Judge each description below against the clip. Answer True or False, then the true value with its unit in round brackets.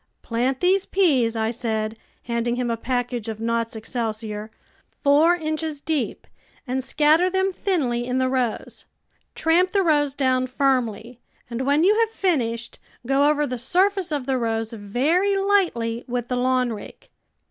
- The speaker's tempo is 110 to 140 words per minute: False (165 wpm)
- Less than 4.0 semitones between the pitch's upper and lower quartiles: False (5.2 semitones)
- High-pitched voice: True (255 Hz)